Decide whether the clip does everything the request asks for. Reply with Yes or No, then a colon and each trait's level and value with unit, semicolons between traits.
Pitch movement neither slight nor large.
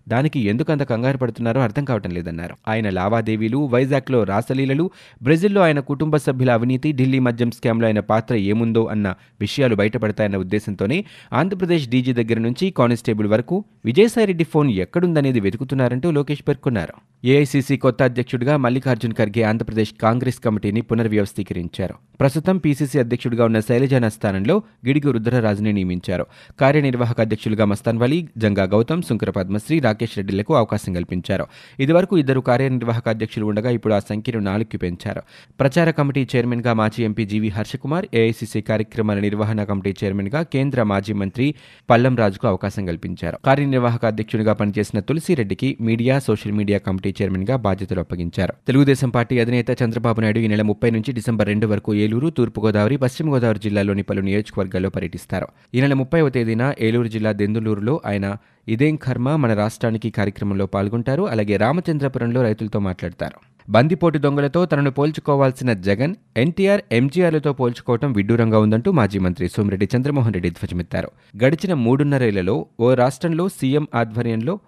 Yes: average, 4.4 semitones